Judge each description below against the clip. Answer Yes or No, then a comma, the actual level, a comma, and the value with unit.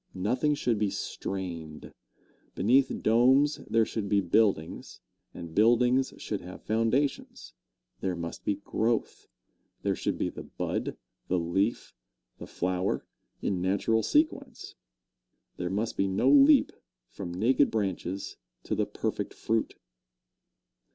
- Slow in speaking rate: Yes, slow, 125 wpm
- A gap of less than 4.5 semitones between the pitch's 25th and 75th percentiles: No, average, 4.8 semitones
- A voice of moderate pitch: No, low, 105 Hz